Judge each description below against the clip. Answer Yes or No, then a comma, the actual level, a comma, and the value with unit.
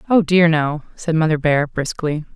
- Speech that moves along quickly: No, average, 180 wpm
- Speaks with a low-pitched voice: No, medium, 160 Hz